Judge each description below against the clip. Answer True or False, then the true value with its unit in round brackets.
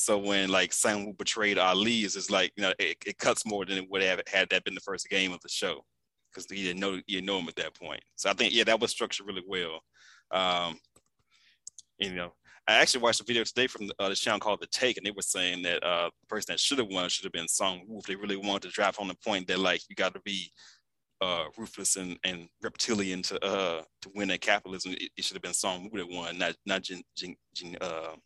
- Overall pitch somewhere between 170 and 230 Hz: False (95 Hz)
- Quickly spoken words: True (255 wpm)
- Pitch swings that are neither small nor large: False (2.1 semitones)